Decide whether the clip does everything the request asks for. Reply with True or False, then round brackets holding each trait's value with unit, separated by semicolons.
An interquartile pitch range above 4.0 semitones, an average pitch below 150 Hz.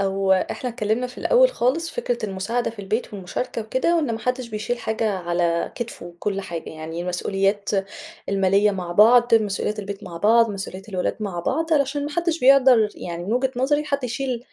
False (4.7 semitones; 220 Hz)